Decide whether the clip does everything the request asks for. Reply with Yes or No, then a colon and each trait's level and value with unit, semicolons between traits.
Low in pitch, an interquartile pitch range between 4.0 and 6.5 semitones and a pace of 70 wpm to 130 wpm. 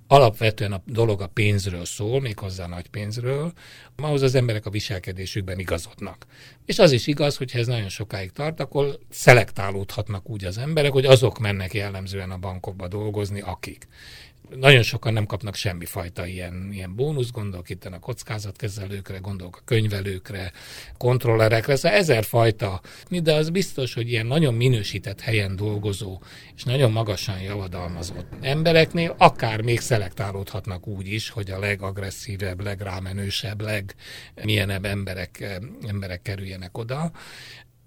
No: low, 105 Hz; average, 4.3 semitones; average, 140 wpm